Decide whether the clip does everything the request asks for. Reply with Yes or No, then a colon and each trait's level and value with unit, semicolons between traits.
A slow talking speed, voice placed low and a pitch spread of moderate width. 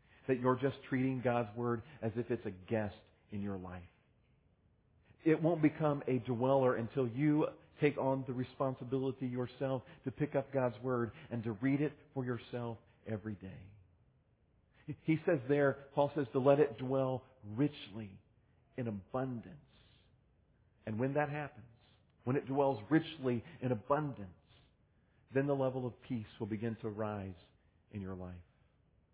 No: average, 150 wpm; low, 125 Hz; average, 3.8 semitones